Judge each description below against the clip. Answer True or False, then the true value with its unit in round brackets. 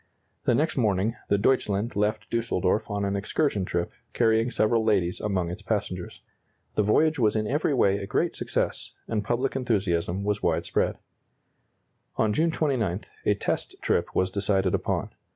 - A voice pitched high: False (105 Hz)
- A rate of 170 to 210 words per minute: False (155 wpm)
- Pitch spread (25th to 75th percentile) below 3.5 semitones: True (3.1 semitones)